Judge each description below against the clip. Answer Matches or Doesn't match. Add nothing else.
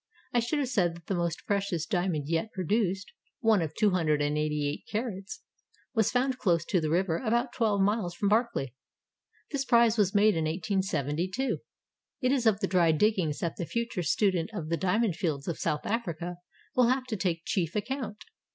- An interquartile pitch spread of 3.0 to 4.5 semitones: Doesn't match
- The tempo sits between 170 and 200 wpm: Matches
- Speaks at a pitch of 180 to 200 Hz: Matches